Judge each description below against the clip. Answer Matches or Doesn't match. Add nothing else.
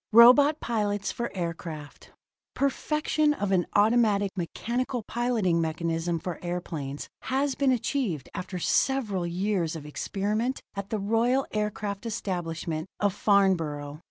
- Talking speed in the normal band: Doesn't match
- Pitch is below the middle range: Doesn't match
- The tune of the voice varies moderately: Doesn't match